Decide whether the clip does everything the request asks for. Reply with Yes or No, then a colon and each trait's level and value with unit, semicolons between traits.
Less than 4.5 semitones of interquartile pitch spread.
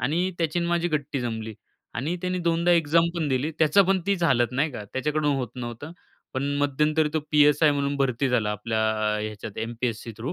No: average, 4.9 semitones